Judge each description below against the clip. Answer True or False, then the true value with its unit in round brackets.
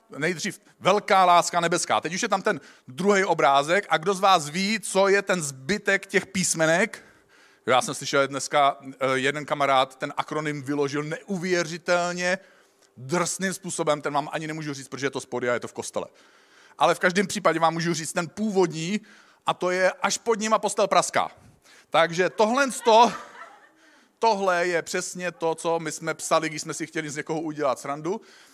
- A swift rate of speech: True (175 wpm)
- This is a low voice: False (170 Hz)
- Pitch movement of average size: True (4.7 semitones)